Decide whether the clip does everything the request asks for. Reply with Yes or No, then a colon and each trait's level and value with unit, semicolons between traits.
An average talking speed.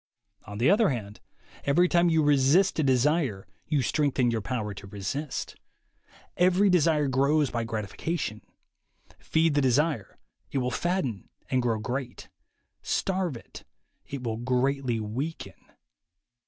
No: slow, 130 wpm